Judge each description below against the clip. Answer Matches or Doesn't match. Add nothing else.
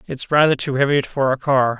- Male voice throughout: Matches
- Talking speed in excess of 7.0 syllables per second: Doesn't match